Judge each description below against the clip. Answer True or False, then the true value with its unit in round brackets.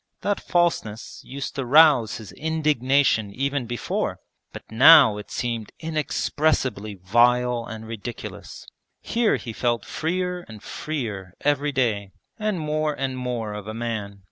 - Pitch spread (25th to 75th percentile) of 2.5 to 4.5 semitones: False (5.6 semitones)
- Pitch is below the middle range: True (125 Hz)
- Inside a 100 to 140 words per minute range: True (135 wpm)